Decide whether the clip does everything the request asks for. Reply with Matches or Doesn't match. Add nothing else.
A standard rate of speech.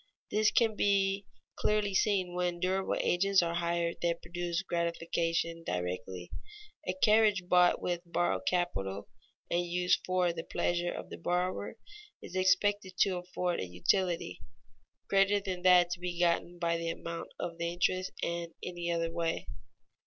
Matches